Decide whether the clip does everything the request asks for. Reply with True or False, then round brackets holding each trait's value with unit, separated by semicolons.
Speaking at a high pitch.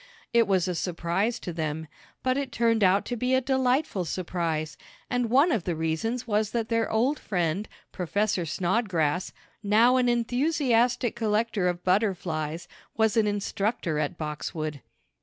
True (205 Hz)